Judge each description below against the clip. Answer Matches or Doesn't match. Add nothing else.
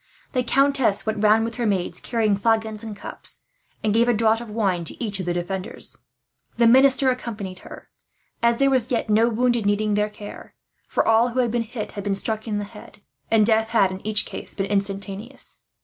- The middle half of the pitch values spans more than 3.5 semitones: Doesn't match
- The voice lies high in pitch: Matches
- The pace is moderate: Doesn't match